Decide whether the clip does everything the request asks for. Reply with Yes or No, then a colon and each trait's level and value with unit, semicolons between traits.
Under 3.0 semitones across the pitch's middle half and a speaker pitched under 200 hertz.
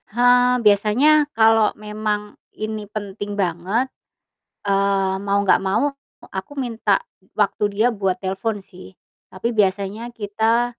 No: narrow, 2.4 semitones; high, 210 Hz